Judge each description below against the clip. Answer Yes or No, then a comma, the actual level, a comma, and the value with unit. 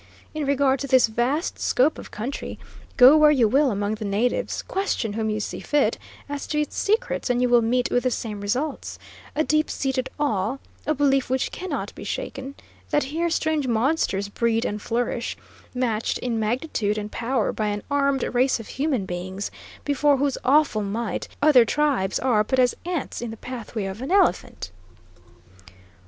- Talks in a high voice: Yes, very high, 250 Hz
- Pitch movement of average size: Yes, average, 4.6 semitones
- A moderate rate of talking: Yes, average, 175 wpm